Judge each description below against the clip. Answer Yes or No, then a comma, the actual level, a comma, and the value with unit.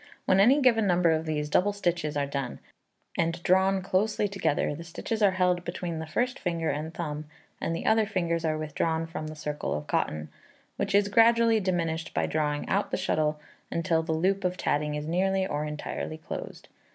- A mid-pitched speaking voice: Yes, medium, 170 Hz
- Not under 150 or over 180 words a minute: No, average, 190 wpm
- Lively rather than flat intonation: No, average, 3.8 semitones